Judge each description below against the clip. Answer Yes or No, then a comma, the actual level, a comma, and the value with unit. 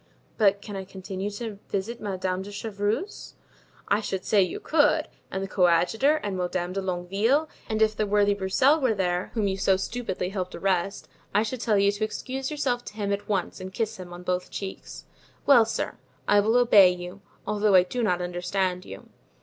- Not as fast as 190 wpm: No, average, 195 wpm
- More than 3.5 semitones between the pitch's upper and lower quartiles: No, average, 2.9 semitones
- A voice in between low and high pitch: No, high, 200 Hz